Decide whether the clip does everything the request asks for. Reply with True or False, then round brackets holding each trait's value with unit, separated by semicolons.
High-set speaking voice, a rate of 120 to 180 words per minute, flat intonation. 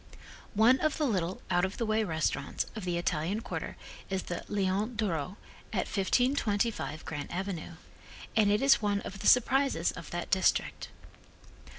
False (200 Hz; 160 wpm; 4.2 semitones)